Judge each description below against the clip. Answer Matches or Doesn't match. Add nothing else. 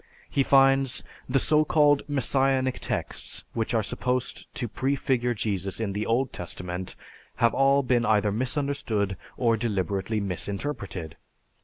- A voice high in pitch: Doesn't match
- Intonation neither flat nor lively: Matches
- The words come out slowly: Matches